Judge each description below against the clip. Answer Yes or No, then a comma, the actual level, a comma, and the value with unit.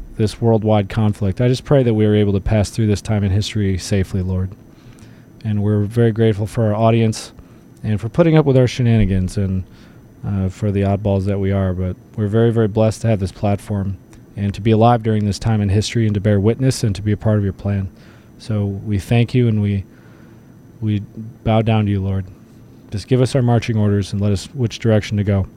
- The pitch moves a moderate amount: No, narrow, 2.3 semitones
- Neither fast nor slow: No, fast, 225 wpm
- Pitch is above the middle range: No, low, 105 Hz